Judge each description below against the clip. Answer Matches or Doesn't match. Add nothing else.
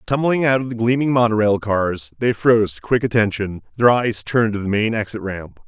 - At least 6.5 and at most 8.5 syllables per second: Doesn't match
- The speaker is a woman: Doesn't match